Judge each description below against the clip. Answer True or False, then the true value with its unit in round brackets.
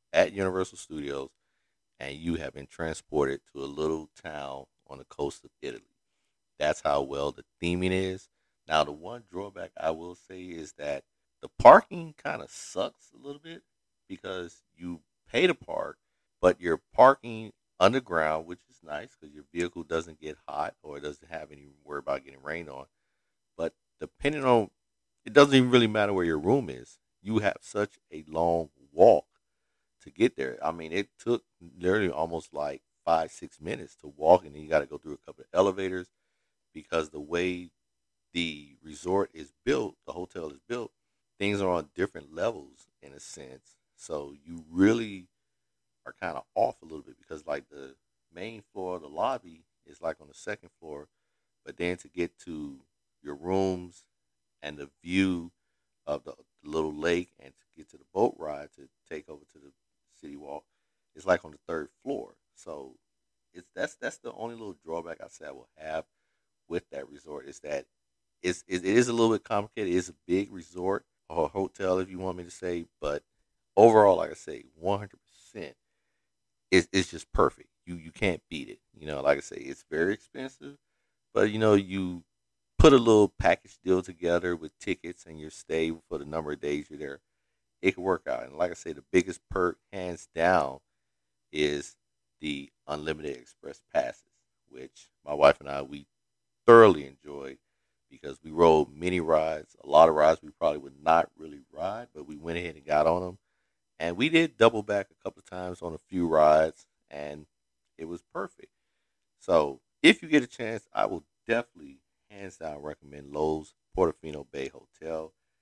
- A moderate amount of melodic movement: True (4.2 semitones)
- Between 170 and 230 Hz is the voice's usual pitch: False (85 Hz)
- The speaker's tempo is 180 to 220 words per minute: True (185 wpm)